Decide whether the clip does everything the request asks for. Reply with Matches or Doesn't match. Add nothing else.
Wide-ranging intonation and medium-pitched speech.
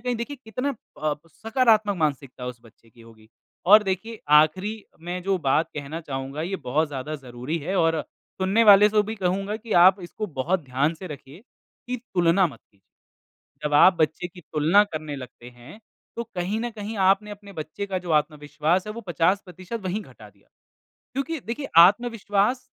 Matches